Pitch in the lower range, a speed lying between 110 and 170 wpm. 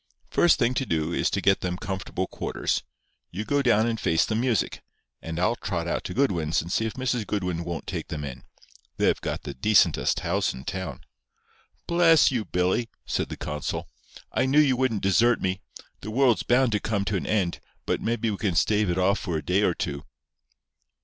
No: low, 100 Hz; fast, 205 wpm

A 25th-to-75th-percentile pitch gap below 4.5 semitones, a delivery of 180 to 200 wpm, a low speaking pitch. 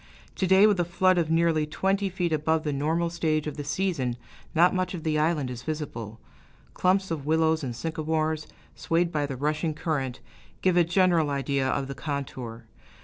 No: average, 3.3 semitones; average, 185 wpm; medium, 155 Hz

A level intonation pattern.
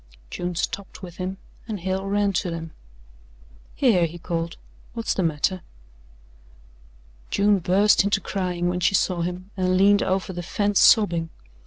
Yes: narrow, 2.3 semitones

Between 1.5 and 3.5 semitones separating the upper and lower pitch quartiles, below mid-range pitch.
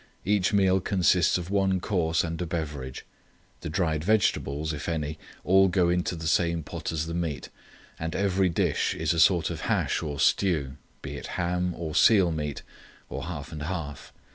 Yes: average, 2.8 semitones; very low, 85 Hz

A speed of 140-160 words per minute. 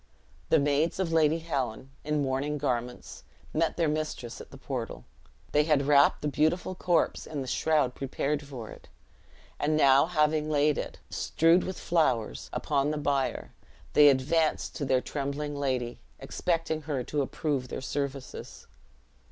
Yes: average, 150 wpm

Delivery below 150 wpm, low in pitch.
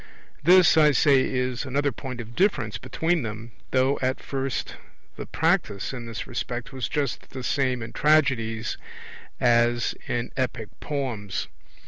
Yes: average, 140 wpm; low, 130 Hz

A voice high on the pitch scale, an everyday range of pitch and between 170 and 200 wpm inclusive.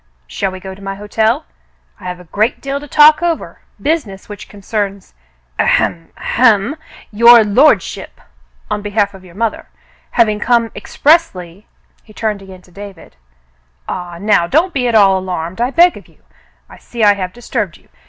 Yes: high, 205 Hz; average, 4.1 semitones; average, 190 wpm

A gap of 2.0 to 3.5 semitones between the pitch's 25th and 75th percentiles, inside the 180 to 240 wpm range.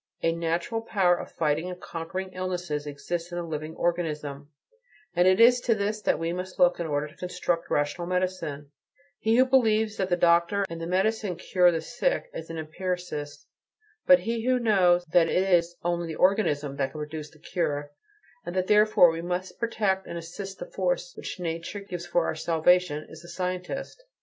Yes: average, 2.9 semitones; average, 190 wpm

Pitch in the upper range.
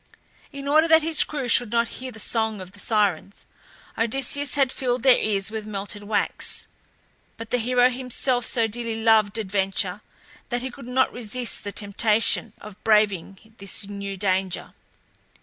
Yes: high, 225 Hz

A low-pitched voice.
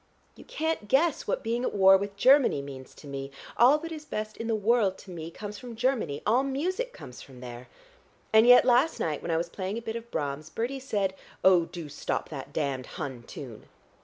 No: high, 205 Hz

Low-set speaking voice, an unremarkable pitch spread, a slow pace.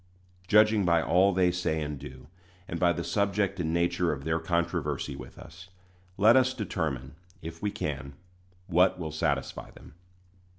No: very low, 85 Hz; average, 3.6 semitones; average, 160 wpm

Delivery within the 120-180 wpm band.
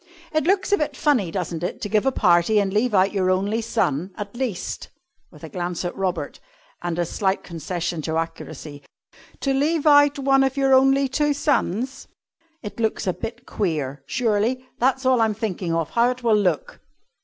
No: average, 190 wpm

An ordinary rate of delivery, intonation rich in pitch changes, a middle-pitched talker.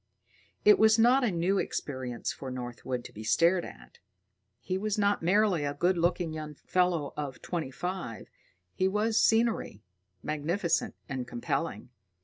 Yes: average, 145 wpm; wide, 6.3 semitones; medium, 170 Hz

